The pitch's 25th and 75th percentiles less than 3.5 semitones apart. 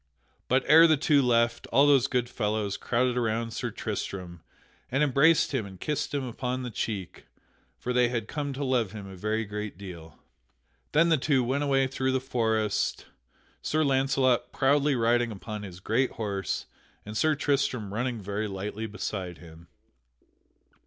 No: average, 4.3 semitones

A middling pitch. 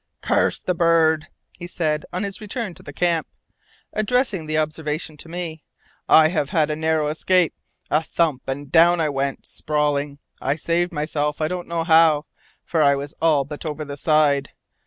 Yes: medium, 155 Hz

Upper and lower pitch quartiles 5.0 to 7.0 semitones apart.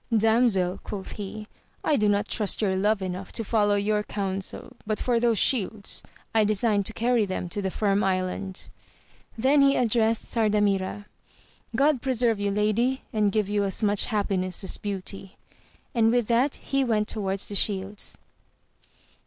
No: narrow, 2.6 semitones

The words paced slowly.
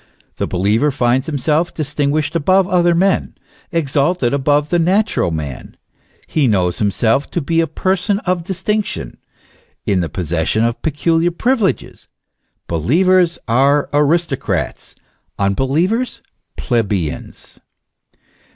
Yes: slow, 110 wpm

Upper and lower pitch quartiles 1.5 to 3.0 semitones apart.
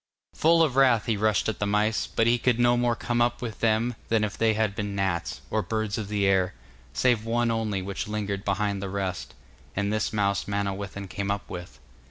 Yes: narrow, 2.4 semitones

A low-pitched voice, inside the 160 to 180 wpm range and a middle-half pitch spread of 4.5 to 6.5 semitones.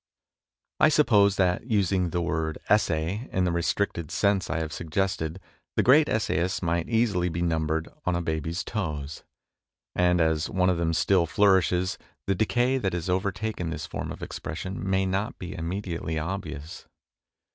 No: very low, 90 Hz; average, 165 wpm; average, 3.3 semitones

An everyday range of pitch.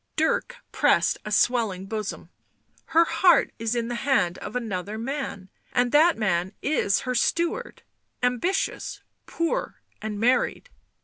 No: wide, 6.0 semitones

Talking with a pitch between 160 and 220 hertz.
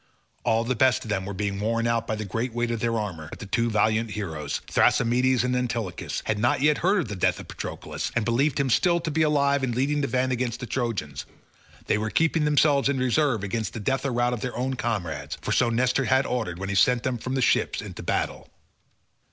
No: low, 120 Hz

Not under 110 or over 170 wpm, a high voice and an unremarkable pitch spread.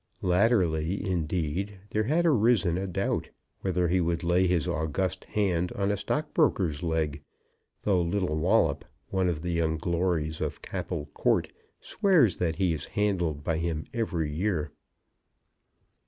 No: average, 140 wpm; very low, 90 Hz; average, 3.6 semitones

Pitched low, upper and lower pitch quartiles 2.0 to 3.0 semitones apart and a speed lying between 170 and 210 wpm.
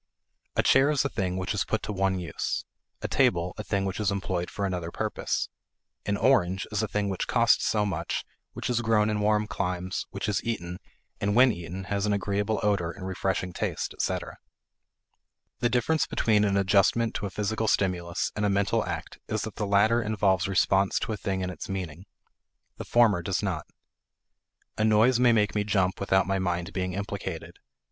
Yes: low, 100 Hz; narrow, 2.4 semitones; average, 195 wpm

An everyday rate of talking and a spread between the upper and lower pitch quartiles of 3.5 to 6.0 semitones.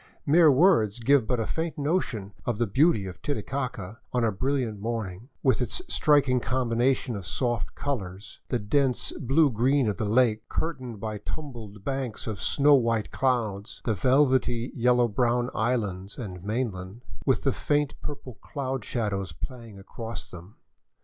Yes: average, 160 wpm; average, 4.1 semitones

